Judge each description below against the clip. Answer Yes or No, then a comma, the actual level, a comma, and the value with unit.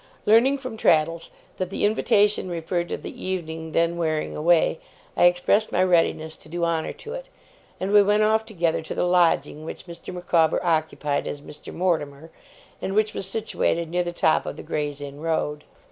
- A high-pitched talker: No, medium, 170 Hz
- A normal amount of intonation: Yes, average, 3.3 semitones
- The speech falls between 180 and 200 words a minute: Yes, average, 185 wpm